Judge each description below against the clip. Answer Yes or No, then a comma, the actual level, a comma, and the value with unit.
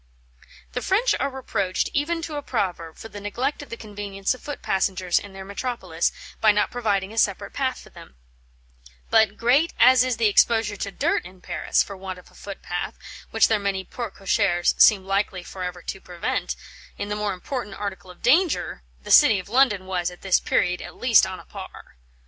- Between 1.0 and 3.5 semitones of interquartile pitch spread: No, average, 4.4 semitones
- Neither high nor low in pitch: No, high, 205 Hz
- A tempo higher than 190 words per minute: Yes, average, 200 wpm